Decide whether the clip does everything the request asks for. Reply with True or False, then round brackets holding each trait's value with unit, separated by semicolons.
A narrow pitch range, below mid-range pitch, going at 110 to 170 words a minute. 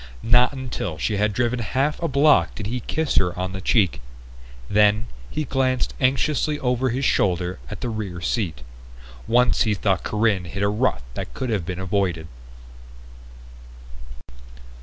False (5.3 semitones; 110 Hz; 155 wpm)